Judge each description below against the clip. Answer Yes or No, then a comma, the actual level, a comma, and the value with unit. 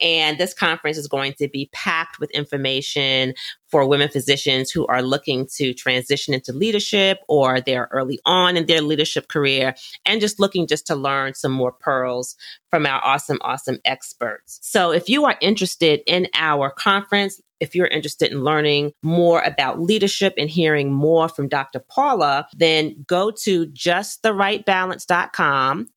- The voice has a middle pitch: Yes, medium, 150 Hz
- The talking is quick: No, average, 155 wpm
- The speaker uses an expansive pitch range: No, average, 4.6 semitones